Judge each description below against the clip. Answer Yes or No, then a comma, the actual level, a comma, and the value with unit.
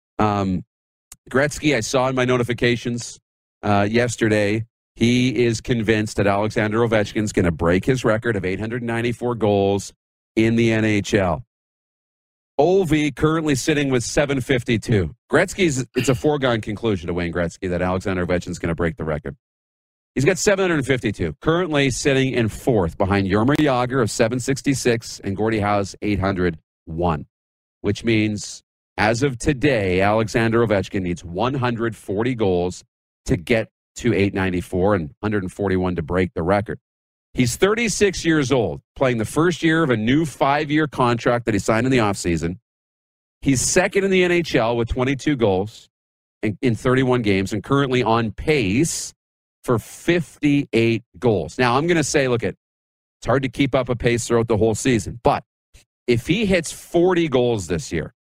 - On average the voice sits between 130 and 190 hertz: No, low, 115 Hz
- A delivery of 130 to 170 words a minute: Yes, average, 150 wpm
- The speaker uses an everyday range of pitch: No, wide, 5.7 semitones